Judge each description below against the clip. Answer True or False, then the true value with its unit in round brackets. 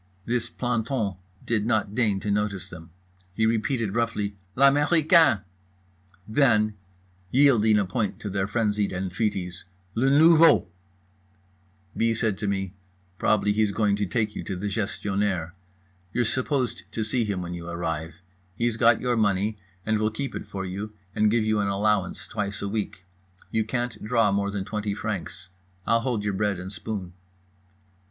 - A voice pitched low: True (105 Hz)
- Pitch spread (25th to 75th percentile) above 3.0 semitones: False (2.7 semitones)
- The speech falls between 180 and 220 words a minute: False (160 wpm)